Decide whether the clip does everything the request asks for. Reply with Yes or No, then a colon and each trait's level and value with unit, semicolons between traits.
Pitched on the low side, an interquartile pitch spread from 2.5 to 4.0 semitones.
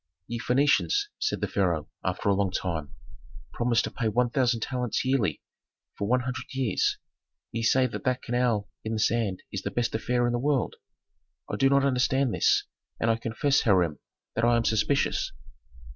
Yes: low, 120 Hz; average, 2.9 semitones